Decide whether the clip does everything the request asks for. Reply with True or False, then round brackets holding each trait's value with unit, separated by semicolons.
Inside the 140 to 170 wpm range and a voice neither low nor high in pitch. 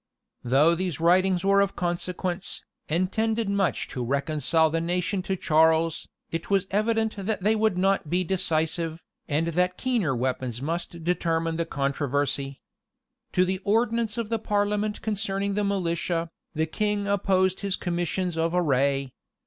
True (150 wpm; 180 Hz)